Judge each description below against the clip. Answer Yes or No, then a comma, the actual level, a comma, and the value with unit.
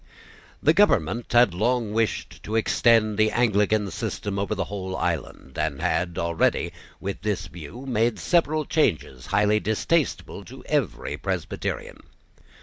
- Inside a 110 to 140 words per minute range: Yes, slow, 135 wpm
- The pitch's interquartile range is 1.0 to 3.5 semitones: No, average, 4.2 semitones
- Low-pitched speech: Yes, low, 105 Hz